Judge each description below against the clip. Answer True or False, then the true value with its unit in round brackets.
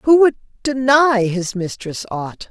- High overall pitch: True (225 Hz)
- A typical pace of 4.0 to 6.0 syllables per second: False (3.7 syllables/s)